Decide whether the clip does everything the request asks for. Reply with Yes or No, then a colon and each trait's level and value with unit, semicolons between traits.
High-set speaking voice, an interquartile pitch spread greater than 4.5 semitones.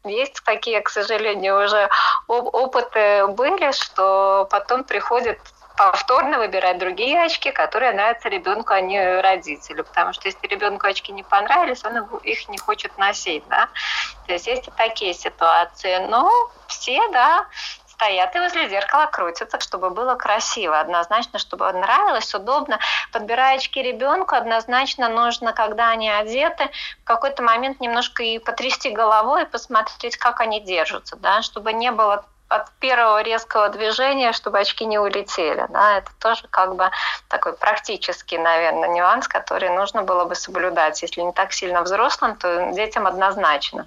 Yes: high, 225 Hz; average, 5.1 semitones